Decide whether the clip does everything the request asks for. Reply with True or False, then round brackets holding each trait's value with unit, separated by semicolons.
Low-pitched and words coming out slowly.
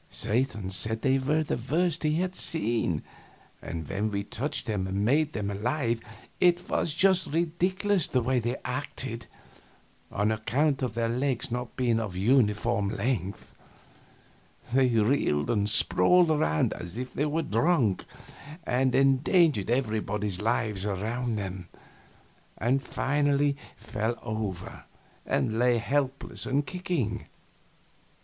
True (120 Hz; 130 wpm)